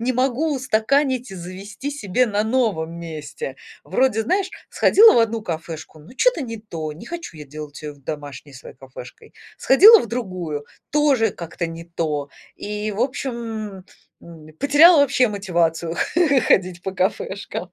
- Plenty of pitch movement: Yes, wide, 7.6 semitones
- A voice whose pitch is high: Yes, high, 205 Hz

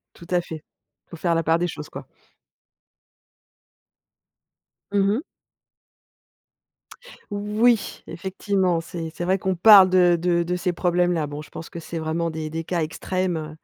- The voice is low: No, medium, 175 Hz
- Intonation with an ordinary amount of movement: No, narrow, 2.3 semitones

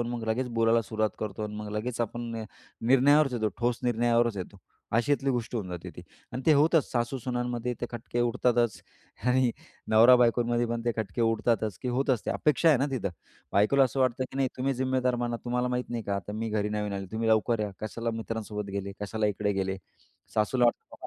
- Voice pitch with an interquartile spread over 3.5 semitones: No, narrow, 2.6 semitones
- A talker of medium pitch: No, low, 120 Hz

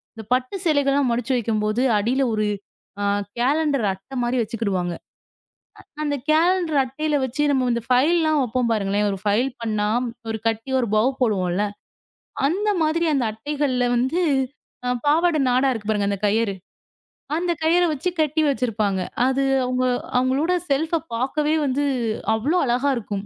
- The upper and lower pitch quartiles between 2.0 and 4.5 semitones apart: No, average, 5.1 semitones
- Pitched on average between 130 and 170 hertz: No, very high, 255 Hz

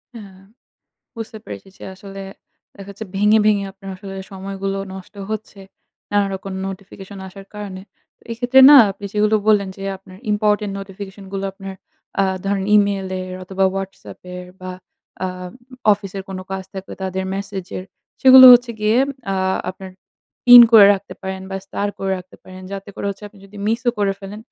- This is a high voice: Yes, high, 195 Hz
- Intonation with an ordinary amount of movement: No, narrow, 1.4 semitones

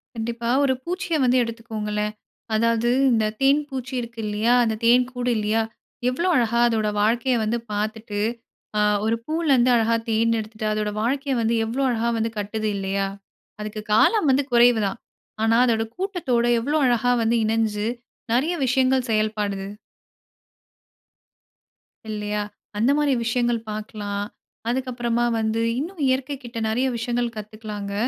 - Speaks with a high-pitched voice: Yes, high, 230 Hz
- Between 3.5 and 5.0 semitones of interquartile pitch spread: No, average, 2.8 semitones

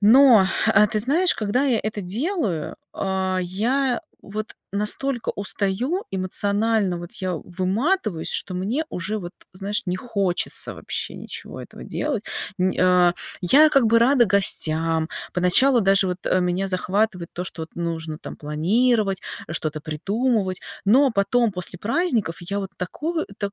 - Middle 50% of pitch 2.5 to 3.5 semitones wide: No, average, 4.7 semitones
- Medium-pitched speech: No, high, 200 Hz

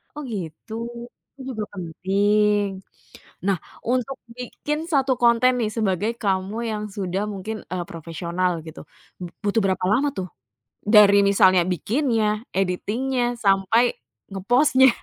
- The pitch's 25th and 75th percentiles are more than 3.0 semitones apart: Yes, average, 4.2 semitones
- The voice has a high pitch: Yes, high, 210 Hz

